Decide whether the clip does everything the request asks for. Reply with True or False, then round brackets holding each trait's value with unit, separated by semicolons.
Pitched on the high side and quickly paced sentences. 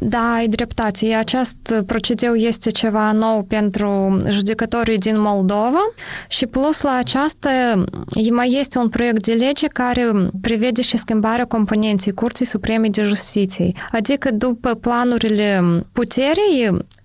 False (230 Hz; 125 wpm)